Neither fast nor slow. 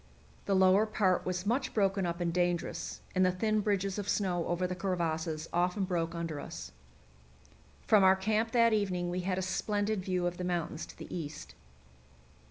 Yes: average, 180 wpm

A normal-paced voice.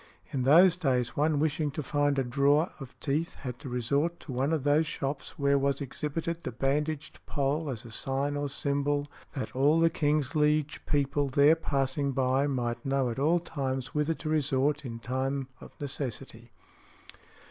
Yes: average, 175 wpm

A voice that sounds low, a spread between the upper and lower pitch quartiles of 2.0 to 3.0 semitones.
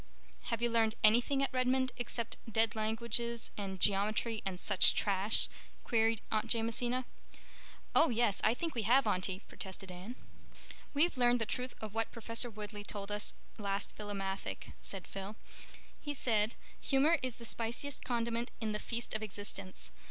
No: high, 225 Hz; average, 2.7 semitones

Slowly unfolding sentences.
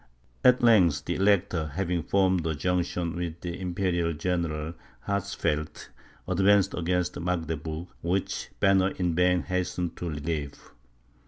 Yes: slow, 120 wpm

